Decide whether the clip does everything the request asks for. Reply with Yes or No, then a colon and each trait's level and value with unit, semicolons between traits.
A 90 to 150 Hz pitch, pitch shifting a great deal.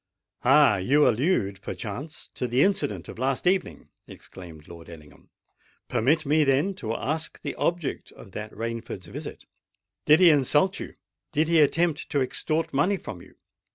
Yes: low, 135 Hz; wide, 7.0 semitones